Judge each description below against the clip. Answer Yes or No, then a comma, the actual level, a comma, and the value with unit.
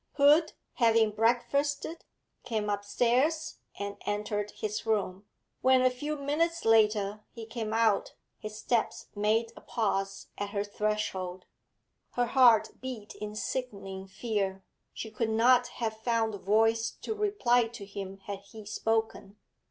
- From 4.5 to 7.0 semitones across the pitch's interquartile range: No, average, 3.0 semitones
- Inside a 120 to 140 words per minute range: Yes, slow, 135 wpm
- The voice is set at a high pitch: Yes, high, 220 Hz